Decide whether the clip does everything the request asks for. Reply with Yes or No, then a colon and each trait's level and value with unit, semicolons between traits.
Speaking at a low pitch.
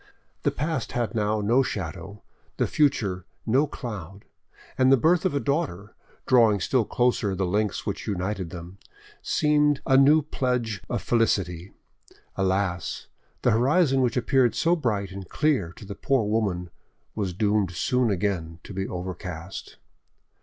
Yes: low, 105 Hz